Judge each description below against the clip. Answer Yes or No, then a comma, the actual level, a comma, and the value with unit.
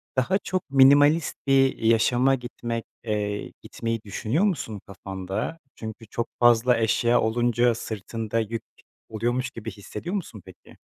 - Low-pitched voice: Yes, low, 115 Hz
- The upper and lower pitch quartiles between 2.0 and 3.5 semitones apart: Yes, average, 3.1 semitones